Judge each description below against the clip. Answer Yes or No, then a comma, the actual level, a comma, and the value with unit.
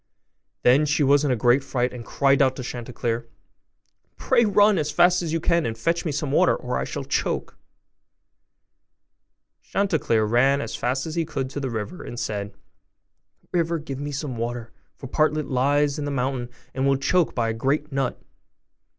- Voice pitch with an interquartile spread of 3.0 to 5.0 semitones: Yes, average, 3.9 semitones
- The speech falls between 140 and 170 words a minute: No, average, 190 wpm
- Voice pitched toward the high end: No, medium, 140 Hz